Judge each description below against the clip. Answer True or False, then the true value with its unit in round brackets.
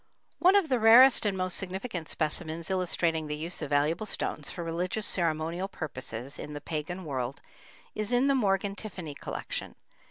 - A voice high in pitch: False (175 Hz)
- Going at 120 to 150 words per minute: False (165 wpm)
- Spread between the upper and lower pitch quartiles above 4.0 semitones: True (4.8 semitones)